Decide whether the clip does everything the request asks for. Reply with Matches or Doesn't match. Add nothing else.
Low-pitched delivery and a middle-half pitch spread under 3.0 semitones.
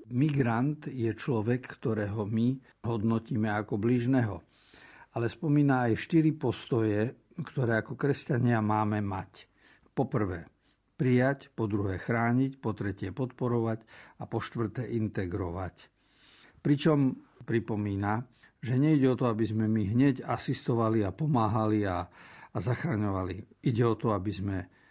Doesn't match